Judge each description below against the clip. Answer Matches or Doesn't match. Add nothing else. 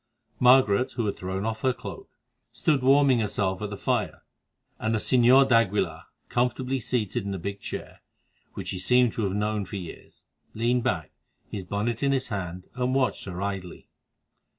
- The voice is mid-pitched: Doesn't match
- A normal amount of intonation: Matches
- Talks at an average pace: Matches